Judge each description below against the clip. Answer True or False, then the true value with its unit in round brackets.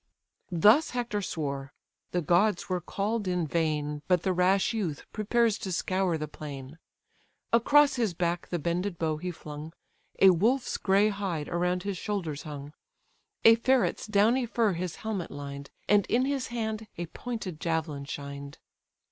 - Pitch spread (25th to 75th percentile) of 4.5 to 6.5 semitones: True (5.4 semitones)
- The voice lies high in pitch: False (180 Hz)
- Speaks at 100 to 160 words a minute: True (155 wpm)